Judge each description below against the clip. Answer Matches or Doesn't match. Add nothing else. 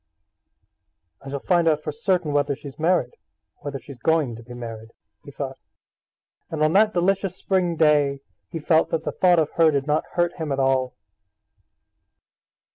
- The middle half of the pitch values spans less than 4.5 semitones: Matches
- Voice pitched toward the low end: Doesn't match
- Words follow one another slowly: Doesn't match